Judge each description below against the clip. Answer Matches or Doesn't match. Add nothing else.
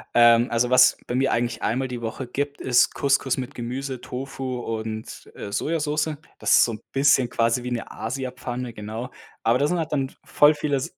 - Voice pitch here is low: Matches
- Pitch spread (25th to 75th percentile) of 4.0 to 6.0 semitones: Doesn't match